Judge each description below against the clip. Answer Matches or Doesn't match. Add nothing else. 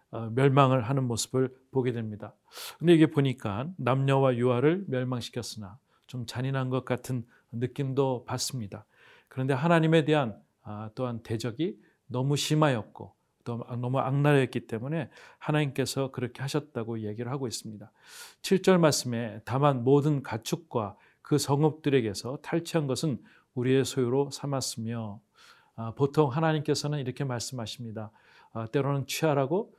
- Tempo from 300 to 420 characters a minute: Matches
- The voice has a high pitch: Doesn't match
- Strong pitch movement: Doesn't match